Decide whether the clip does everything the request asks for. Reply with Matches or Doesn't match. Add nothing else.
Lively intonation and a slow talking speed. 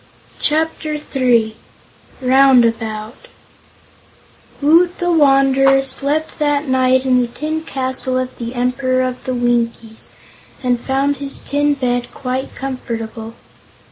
Doesn't match